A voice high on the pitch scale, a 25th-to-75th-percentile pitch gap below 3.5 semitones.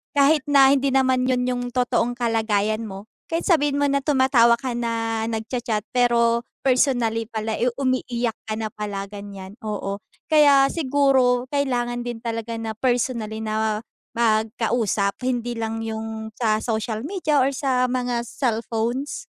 Yes: high, 235 Hz; average, 2.8 semitones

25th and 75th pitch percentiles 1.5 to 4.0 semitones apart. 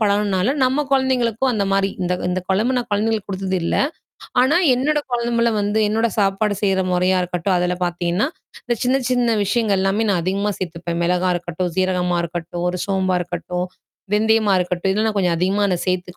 Yes: average, 3.7 semitones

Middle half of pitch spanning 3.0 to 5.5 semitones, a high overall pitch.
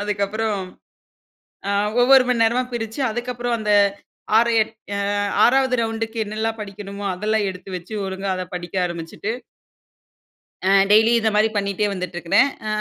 No: narrow, 2.5 semitones; high, 215 Hz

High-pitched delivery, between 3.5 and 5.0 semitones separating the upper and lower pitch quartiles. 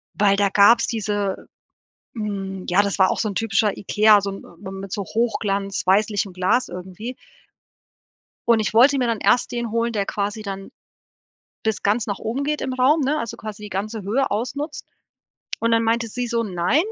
No: high, 215 Hz; average, 2.9 semitones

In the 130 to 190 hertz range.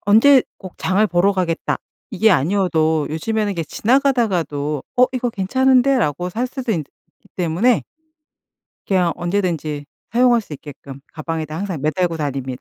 Yes: medium, 185 Hz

